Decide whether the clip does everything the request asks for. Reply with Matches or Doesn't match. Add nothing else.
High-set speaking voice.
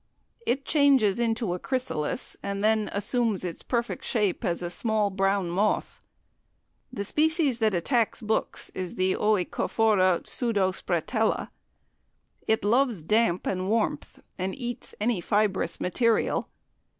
Matches